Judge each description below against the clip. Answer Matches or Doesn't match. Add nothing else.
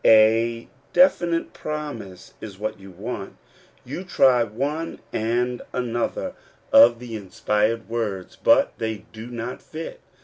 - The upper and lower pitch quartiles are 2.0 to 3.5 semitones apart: Matches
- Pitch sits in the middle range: Doesn't match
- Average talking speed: Doesn't match